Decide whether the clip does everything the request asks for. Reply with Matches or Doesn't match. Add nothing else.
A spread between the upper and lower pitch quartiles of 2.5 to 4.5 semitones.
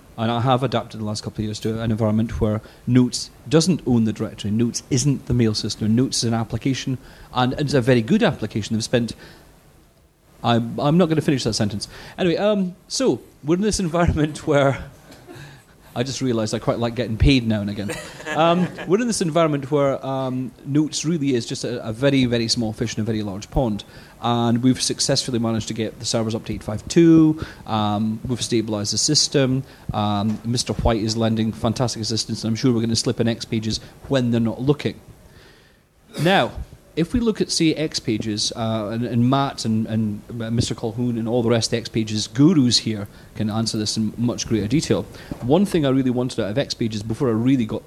Matches